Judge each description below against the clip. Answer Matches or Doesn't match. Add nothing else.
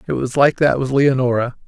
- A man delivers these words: Matches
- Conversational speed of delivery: Doesn't match